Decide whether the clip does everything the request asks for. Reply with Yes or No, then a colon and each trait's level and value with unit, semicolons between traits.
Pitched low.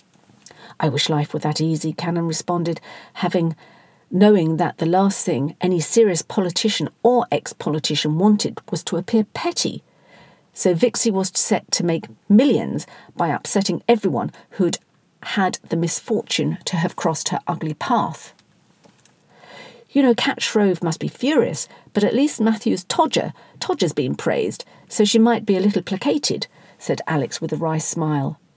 No: medium, 180 Hz